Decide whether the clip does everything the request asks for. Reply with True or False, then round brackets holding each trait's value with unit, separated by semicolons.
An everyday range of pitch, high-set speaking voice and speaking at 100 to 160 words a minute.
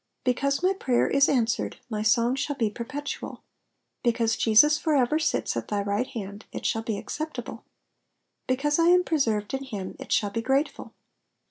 False (4.6 semitones; 250 Hz; 175 wpm)